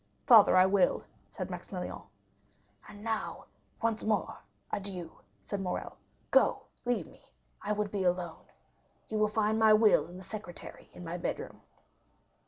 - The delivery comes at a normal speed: Yes, average, 145 wpm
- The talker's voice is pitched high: Yes, high, 205 Hz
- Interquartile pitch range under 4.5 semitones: Yes, average, 2.9 semitones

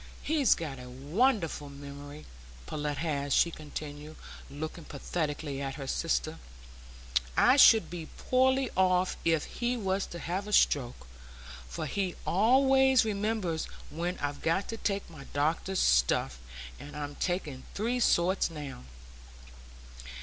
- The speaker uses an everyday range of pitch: No, wide, 5.7 semitones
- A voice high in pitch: No, medium, 165 Hz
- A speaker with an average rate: No, slow, 130 wpm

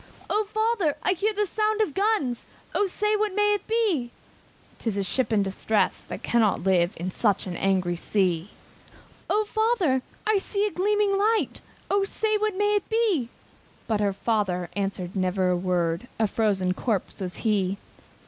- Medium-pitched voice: No, high, 245 Hz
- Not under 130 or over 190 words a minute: Yes, average, 165 wpm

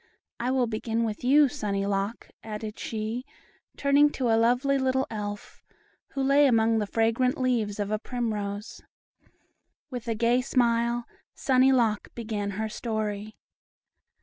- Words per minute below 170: Yes, average, 140 wpm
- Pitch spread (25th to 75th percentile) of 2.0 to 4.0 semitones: Yes, average, 2.9 semitones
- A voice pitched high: Yes, high, 230 Hz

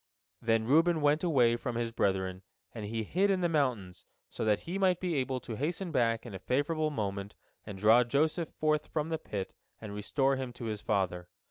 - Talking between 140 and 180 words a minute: No, fast, 205 wpm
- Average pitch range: No, wide, 6.5 semitones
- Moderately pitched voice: No, low, 125 Hz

